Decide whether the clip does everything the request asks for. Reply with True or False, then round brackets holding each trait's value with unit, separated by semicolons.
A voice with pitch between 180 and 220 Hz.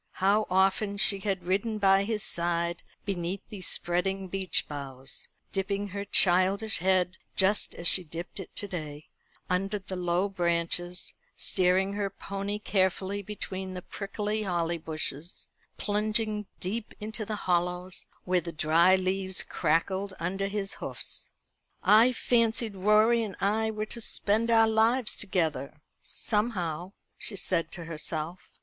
True (190 Hz)